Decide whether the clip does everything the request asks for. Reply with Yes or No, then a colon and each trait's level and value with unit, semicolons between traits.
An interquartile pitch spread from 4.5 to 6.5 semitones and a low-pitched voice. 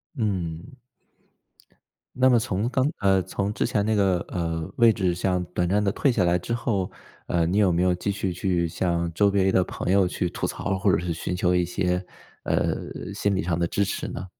No: narrow, 2.4 semitones; very low, 95 Hz